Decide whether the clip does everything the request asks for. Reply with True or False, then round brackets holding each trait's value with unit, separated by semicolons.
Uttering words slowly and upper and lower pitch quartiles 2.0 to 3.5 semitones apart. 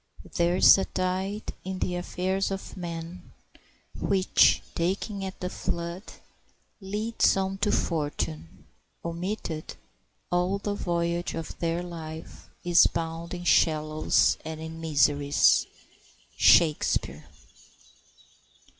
True (110 wpm; 2.7 semitones)